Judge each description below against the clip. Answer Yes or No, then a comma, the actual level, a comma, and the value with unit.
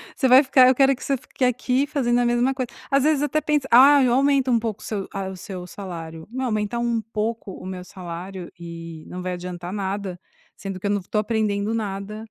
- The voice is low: No, high, 215 Hz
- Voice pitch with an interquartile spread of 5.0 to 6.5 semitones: Yes, average, 5.3 semitones